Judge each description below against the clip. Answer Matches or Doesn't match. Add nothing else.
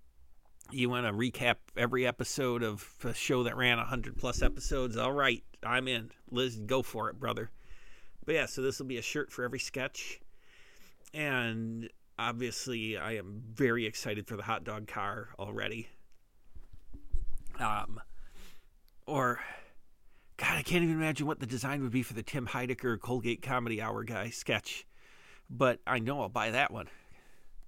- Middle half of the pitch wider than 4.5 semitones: Doesn't match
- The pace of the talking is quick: Doesn't match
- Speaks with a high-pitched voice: Doesn't match